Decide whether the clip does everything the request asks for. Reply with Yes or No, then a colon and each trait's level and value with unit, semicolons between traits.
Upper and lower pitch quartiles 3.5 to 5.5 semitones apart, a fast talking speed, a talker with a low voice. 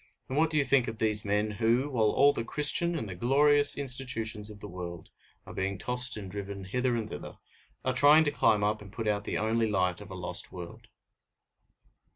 Yes: average, 4.4 semitones; fast, 210 wpm; low, 110 Hz